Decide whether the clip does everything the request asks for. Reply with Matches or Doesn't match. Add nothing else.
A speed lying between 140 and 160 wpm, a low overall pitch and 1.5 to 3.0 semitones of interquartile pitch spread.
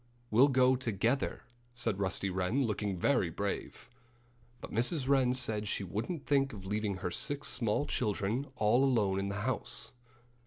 Doesn't match